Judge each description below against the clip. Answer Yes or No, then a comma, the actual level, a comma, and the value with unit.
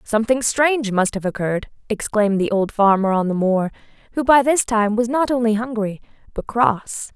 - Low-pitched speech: No, high, 220 Hz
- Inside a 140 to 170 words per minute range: No, average, 185 wpm